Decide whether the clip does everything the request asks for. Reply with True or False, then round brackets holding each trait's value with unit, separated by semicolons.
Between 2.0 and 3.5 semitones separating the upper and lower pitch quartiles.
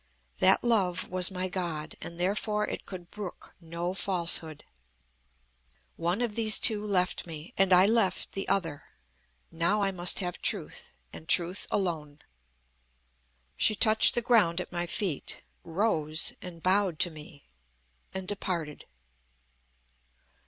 True (3.1 semitones)